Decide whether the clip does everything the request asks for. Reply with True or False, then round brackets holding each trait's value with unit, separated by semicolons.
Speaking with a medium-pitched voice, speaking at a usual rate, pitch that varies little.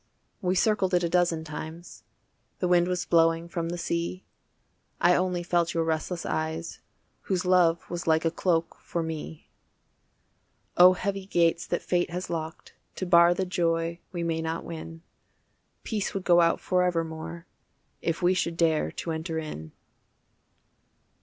True (170 Hz; 155 wpm; 1.5 semitones)